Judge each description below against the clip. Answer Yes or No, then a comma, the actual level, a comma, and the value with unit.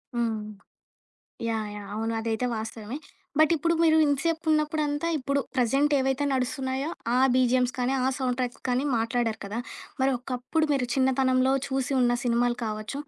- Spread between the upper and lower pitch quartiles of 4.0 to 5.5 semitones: No, average, 2.9 semitones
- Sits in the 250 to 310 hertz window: Yes, very high, 255 Hz